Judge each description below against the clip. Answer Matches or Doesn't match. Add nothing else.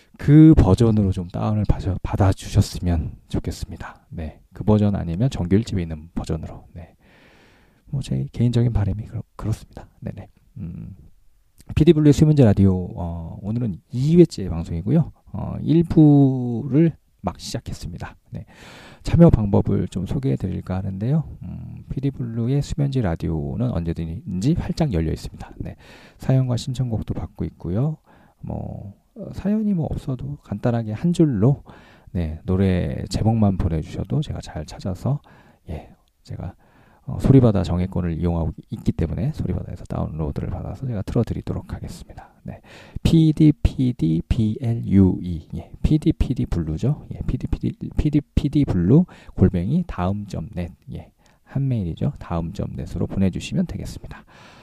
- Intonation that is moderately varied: Doesn't match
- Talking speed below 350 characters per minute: Matches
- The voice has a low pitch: Matches